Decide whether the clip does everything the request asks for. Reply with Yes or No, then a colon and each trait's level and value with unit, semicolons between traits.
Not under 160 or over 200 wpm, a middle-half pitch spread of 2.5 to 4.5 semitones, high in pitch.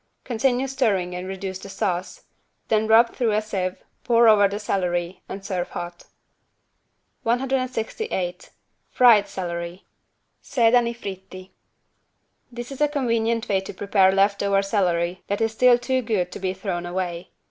No: average, 145 wpm; average, 4.0 semitones; high, 200 Hz